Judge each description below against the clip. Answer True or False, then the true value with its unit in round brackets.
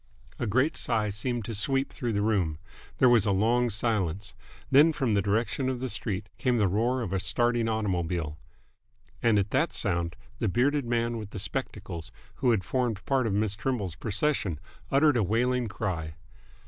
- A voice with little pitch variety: False (3.9 semitones)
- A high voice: False (110 Hz)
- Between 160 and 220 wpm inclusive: True (180 wpm)